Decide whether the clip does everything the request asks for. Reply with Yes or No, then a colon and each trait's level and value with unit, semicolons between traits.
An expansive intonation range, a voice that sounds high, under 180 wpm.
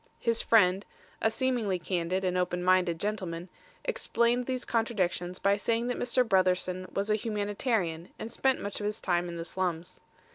No: average, 3.9 semitones; high, 195 Hz; average, 170 wpm